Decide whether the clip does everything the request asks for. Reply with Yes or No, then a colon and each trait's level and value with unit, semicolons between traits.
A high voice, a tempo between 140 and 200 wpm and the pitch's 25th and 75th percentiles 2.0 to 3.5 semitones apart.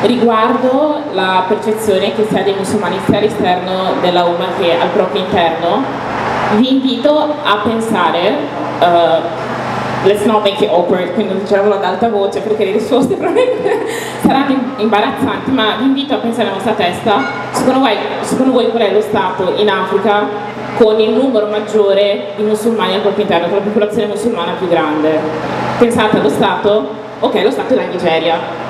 Yes: high, 210 Hz; average, 165 wpm; average, 2.9 semitones